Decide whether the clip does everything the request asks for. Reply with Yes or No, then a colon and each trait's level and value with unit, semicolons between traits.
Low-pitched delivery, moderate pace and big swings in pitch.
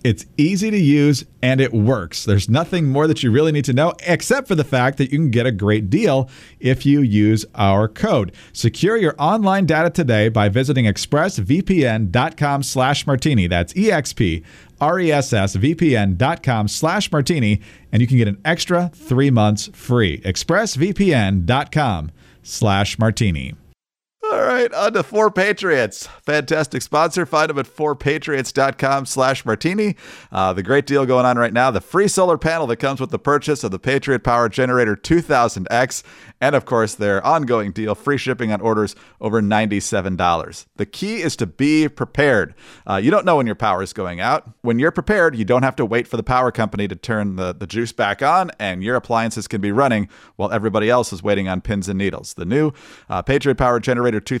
Yes: low, 125 Hz; average, 180 wpm; wide, 5.8 semitones